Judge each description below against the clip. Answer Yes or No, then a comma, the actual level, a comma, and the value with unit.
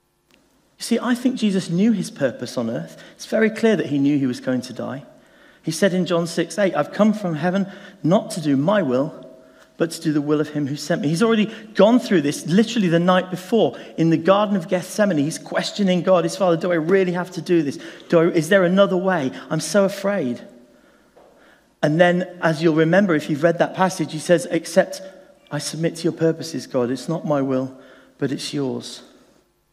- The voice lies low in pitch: No, medium, 175 Hz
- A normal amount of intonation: Yes, average, 3.7 semitones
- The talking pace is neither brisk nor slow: No, fast, 215 wpm